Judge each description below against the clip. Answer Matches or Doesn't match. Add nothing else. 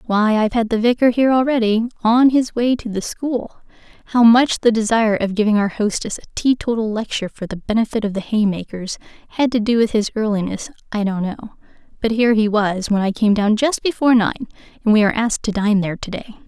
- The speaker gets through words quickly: Matches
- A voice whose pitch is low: Doesn't match